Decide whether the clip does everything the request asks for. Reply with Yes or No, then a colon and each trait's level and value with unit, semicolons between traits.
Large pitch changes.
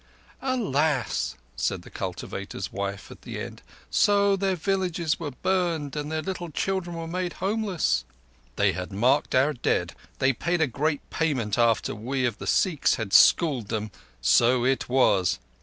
Yes: wide, 7.1 semitones